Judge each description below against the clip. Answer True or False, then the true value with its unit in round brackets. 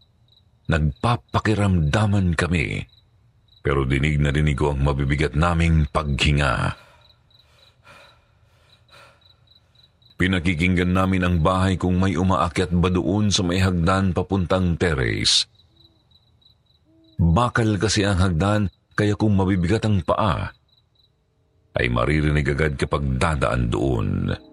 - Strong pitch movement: False (4.6 semitones)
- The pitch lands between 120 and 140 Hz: False (95 Hz)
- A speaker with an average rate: False (100 wpm)